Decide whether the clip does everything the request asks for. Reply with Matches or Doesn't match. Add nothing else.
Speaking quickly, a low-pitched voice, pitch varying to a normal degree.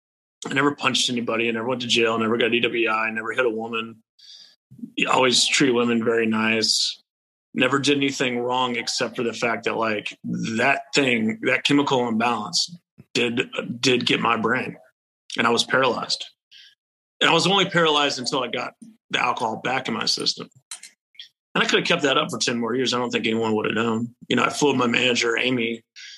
Doesn't match